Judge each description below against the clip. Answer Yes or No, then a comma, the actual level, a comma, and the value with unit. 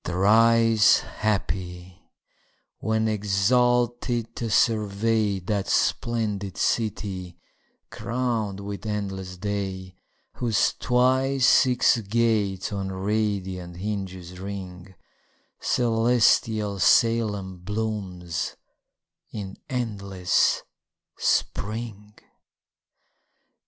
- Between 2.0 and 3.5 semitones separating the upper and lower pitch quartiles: Yes, average, 3.1 semitones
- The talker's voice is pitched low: Yes, low, 105 Hz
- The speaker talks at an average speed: No, slow, 70 wpm